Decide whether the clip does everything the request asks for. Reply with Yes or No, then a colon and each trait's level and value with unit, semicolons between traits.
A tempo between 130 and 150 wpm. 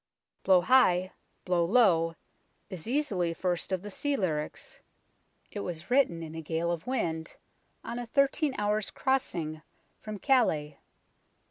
Yes: average, 145 wpm